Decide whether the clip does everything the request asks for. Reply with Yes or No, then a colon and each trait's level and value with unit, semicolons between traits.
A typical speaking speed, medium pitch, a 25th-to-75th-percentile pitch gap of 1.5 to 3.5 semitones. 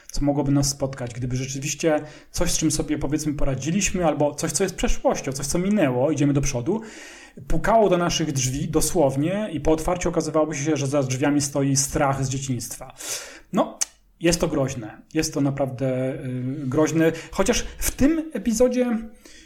No: average, 160 wpm; medium, 155 Hz; average, 4.1 semitones